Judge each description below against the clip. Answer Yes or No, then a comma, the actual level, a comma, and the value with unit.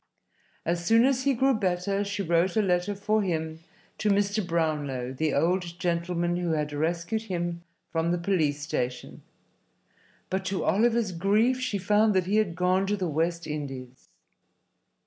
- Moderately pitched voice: Yes, medium, 180 Hz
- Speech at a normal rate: Yes, average, 160 wpm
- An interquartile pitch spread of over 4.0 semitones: No, average, 3.7 semitones